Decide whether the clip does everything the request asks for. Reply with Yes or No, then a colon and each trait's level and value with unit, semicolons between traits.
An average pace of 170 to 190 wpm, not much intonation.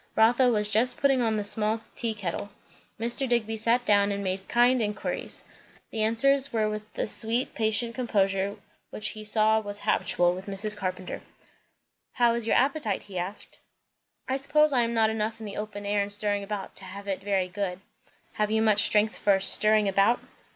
Yes: average, 185 wpm; narrow, 2.3 semitones